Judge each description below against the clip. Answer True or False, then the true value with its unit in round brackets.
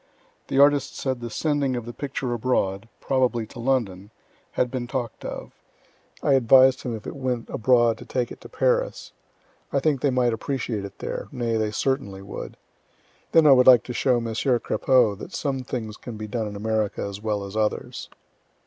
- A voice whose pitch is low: True (120 Hz)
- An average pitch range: True (3.3 semitones)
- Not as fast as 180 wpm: False (190 wpm)